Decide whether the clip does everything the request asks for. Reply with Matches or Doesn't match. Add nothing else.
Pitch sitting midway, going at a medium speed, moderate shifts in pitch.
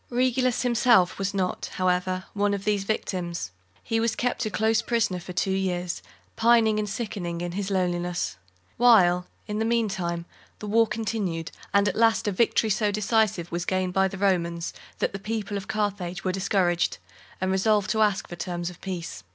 Doesn't match